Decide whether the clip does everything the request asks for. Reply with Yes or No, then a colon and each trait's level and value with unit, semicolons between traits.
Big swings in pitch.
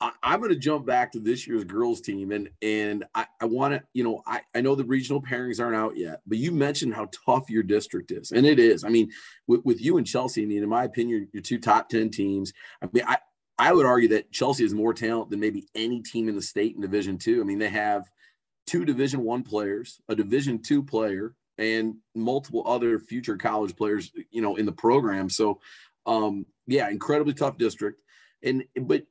No: average, 3.7 semitones